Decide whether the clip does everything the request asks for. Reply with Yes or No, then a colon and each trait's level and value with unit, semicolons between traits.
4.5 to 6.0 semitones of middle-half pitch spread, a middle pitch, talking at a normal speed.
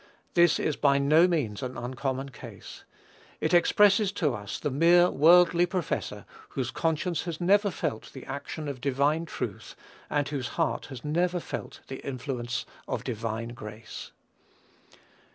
Yes: average, 5.1 semitones; medium, 145 Hz; average, 145 wpm